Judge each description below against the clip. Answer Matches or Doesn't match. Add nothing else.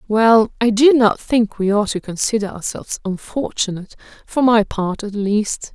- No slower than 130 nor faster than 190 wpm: Matches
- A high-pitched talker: Matches